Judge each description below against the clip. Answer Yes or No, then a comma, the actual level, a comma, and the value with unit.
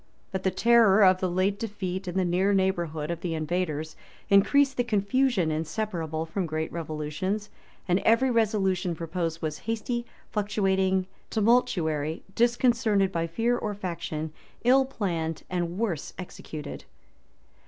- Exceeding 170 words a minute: No, slow, 135 wpm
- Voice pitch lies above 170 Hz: Yes, high, 190 Hz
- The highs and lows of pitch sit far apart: No, average, 4.6 semitones